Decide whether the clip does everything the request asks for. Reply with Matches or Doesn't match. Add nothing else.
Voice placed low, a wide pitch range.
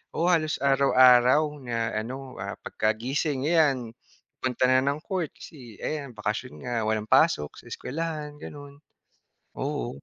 Doesn't match